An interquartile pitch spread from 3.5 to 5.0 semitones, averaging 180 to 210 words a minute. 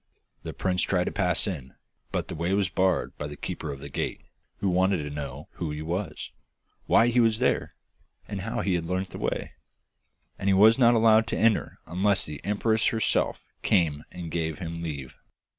Yes: average, 4.6 semitones; average, 195 wpm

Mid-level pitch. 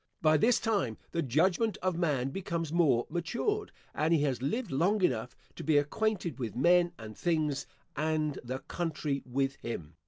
Yes: medium, 155 Hz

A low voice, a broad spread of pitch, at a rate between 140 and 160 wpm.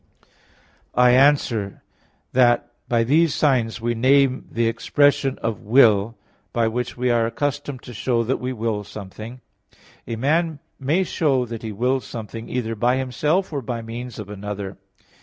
No: low, 120 Hz; average, 2.8 semitones; average, 155 wpm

